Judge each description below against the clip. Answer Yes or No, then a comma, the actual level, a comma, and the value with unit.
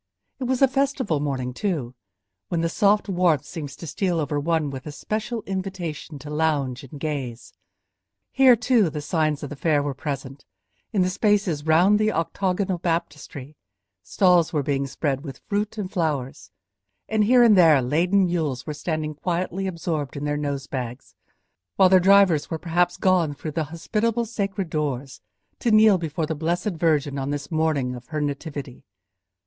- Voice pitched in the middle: Yes, medium, 160 Hz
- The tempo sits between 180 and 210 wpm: No, average, 170 wpm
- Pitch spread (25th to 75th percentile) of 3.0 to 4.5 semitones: No, average, 4.9 semitones